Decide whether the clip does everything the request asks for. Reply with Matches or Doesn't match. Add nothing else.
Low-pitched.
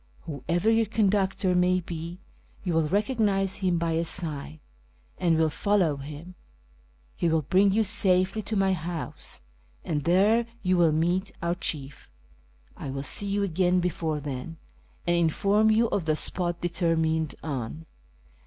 Doesn't match